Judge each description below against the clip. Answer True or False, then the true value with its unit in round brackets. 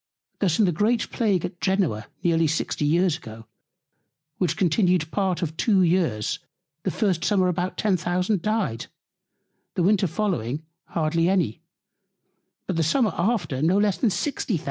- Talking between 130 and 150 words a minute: True (145 wpm)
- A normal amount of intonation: True (3.5 semitones)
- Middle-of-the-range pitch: True (180 Hz)